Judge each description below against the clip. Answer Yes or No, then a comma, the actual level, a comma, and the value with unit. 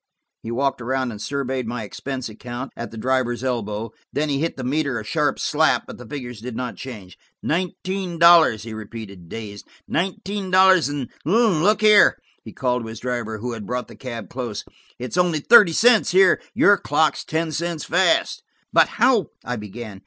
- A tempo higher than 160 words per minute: Yes, average, 180 wpm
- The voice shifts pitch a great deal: Yes, wide, 6.5 semitones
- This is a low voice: Yes, low, 130 Hz